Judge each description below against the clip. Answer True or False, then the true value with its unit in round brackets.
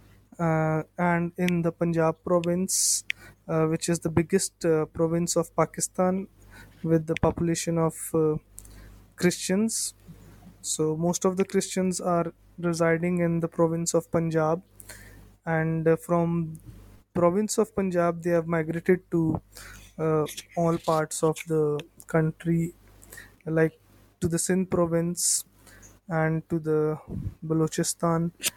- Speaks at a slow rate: True (120 wpm)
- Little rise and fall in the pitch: True (1.7 semitones)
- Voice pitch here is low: False (165 Hz)